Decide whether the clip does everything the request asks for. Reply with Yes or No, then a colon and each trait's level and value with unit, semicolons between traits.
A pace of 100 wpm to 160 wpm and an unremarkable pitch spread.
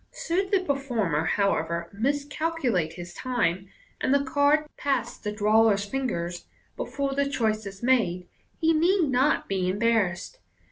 No: average, 140 wpm; wide, 6.6 semitones